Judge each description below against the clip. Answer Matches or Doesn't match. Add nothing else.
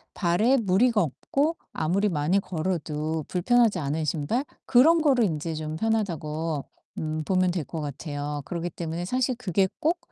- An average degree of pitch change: Doesn't match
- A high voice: Doesn't match